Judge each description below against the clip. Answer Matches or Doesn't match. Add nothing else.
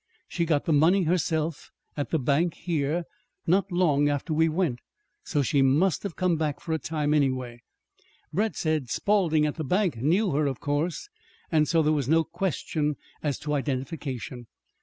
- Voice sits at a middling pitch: Matches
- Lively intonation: Doesn't match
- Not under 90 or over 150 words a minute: Doesn't match